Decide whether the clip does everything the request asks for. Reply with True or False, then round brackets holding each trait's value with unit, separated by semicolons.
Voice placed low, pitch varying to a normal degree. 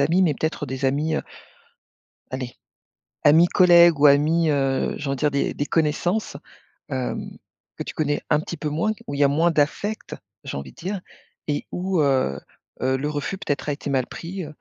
False (150 Hz; 3.4 semitones)